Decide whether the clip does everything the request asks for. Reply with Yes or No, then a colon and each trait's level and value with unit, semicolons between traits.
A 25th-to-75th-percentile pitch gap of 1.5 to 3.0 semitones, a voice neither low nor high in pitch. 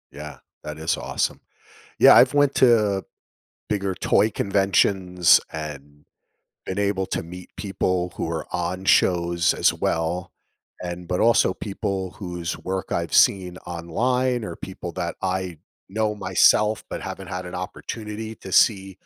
No: average, 2.7 semitones; very low, 95 Hz